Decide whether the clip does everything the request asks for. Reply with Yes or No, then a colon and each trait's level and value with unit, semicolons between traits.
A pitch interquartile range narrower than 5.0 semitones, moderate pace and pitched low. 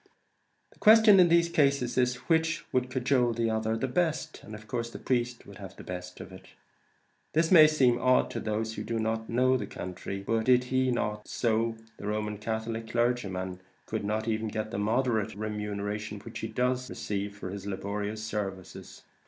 Yes: average, 3.3 semitones; average, 190 wpm; low, 110 Hz